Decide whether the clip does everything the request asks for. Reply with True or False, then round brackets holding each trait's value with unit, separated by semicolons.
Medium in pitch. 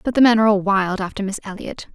False (205 Hz)